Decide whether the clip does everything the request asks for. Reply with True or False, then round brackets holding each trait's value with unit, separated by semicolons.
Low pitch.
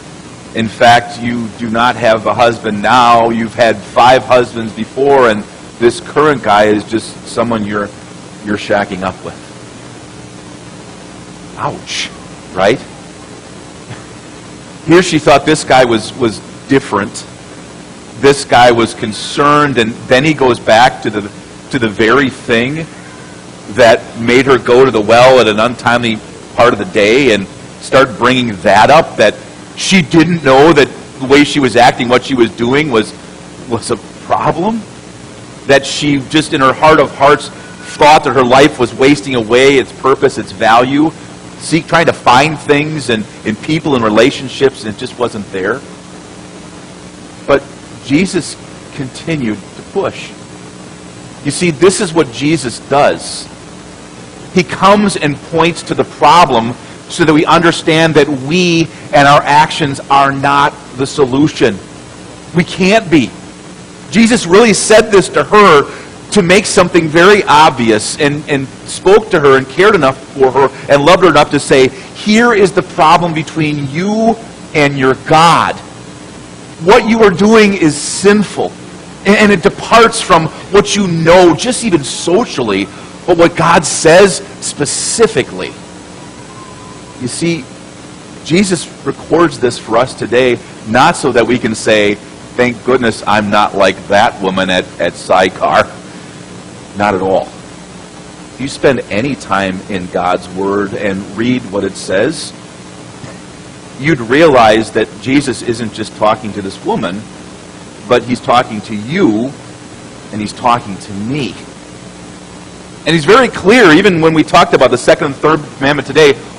True (120 Hz)